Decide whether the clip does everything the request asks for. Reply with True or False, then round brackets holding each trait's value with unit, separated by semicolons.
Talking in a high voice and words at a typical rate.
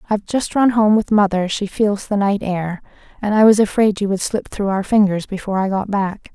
False (200 Hz; 220 wpm)